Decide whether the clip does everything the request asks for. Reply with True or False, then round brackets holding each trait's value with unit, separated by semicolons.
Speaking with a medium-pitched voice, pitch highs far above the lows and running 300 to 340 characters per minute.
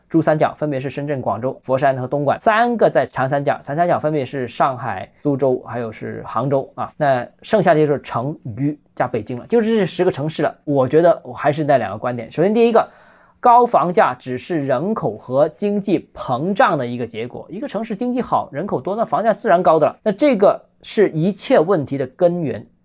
True (145 Hz; 7.7 semitones; 315 characters per minute)